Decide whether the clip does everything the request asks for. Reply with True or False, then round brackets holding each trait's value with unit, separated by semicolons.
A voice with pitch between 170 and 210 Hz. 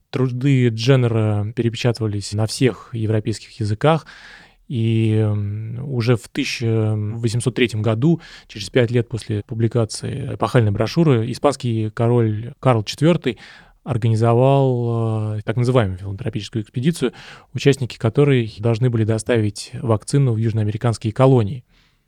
False (115 Hz)